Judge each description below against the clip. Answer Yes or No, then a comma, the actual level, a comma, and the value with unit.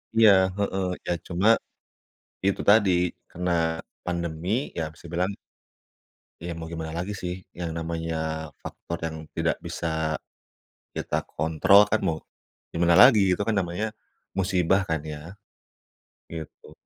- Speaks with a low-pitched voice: Yes, very low, 85 Hz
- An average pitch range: Yes, average, 3.1 semitones